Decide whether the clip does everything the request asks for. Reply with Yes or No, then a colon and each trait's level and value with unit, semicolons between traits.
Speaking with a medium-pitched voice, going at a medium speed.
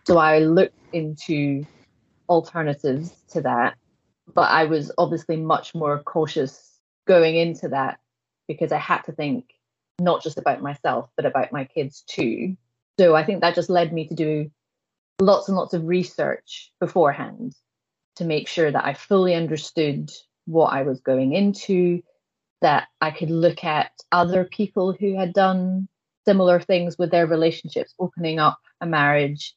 Yes: medium, 165 Hz; average, 155 wpm